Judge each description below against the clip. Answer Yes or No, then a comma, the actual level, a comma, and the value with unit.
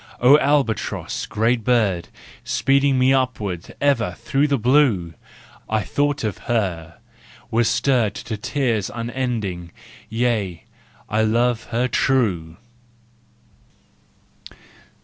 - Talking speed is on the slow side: Yes, slow, 95 wpm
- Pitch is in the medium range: No, low, 115 Hz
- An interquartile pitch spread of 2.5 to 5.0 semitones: Yes, average, 4.1 semitones